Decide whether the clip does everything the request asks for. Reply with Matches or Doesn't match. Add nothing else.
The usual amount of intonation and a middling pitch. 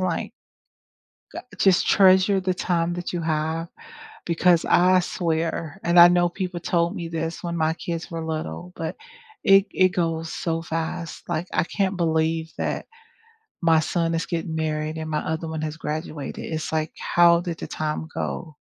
Doesn't match